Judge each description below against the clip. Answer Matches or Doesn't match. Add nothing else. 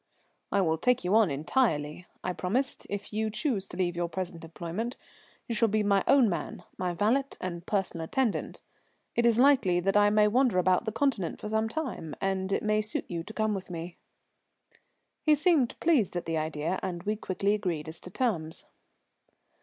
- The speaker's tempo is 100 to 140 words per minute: Doesn't match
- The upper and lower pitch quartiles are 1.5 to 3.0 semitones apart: Doesn't match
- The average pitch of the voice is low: Doesn't match